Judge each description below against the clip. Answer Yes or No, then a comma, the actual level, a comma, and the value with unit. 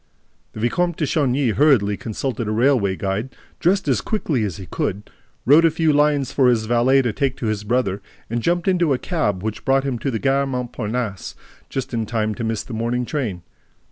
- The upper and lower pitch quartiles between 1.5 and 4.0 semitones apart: No, average, 4.5 semitones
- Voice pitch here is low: Yes, low, 125 Hz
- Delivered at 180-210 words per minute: Yes, fast, 205 wpm